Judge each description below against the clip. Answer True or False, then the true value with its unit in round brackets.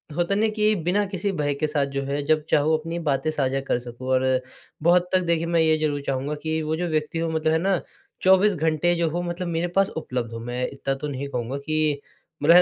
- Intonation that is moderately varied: True (3.6 semitones)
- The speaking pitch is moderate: True (155 Hz)